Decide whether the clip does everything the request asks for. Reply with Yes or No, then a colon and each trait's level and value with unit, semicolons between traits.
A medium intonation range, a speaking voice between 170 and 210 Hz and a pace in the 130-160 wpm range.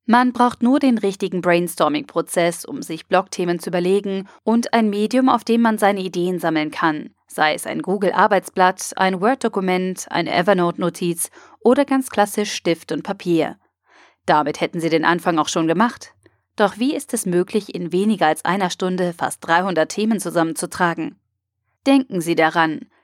Yes: average, 4.2 semitones; medium, 185 Hz; average, 155 wpm